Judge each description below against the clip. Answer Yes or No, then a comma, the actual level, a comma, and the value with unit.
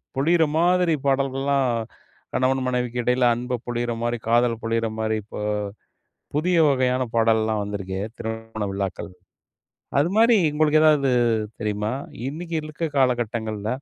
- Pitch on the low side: Yes, low, 125 Hz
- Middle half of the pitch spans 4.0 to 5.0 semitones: Yes, average, 4.3 semitones